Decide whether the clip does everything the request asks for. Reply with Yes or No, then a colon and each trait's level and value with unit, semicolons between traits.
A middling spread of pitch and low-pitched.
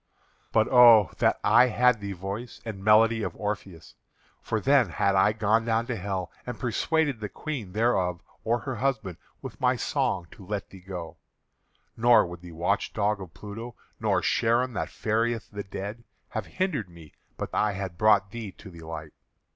Yes: average, 3.5 semitones; low, 105 Hz